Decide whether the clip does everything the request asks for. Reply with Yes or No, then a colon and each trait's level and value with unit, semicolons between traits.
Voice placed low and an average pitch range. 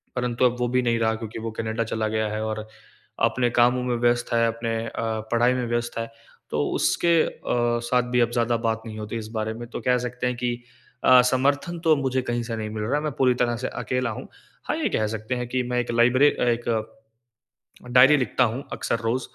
No: low, 120 Hz; narrow, 1.8 semitones